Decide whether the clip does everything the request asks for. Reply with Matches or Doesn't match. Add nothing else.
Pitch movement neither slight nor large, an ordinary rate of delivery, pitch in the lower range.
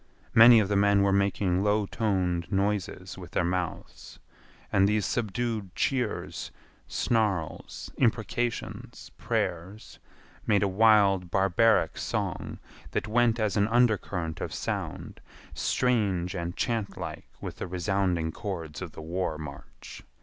Doesn't match